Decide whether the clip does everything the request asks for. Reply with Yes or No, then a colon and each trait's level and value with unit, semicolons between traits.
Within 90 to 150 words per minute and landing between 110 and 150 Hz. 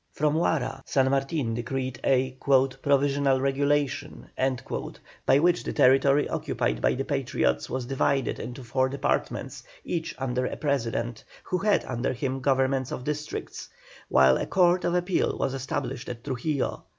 Yes: average, 145 wpm; low, 135 Hz